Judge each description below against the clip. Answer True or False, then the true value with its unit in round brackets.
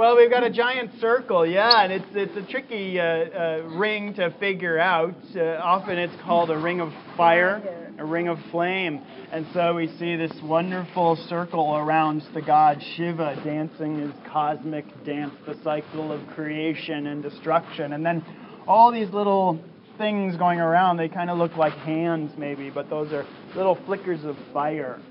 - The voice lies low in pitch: False (170 Hz)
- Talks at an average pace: True (175 wpm)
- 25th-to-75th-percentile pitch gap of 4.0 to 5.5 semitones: False (3.4 semitones)